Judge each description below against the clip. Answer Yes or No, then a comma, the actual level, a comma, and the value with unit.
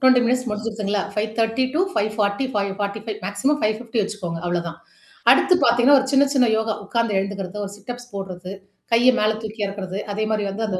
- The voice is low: No, high, 215 Hz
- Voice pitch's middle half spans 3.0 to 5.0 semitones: Yes, average, 3.3 semitones